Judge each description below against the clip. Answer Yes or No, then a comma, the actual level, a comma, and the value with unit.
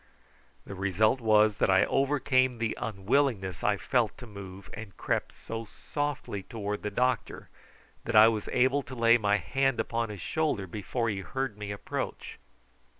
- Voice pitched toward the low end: Yes, low, 110 Hz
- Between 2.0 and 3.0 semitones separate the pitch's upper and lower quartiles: No, average, 3.9 semitones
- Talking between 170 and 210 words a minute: No, average, 160 wpm